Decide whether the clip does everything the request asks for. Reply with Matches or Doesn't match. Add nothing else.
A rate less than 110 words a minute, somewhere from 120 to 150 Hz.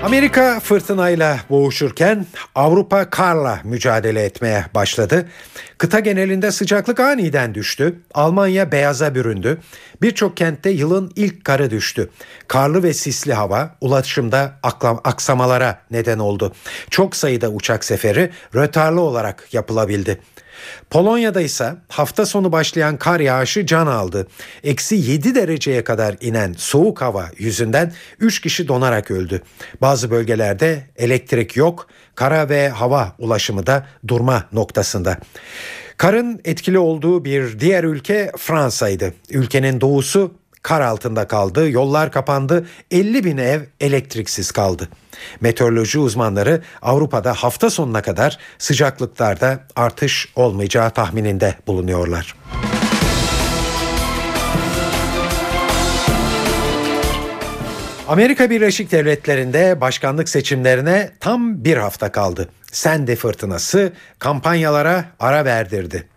Matches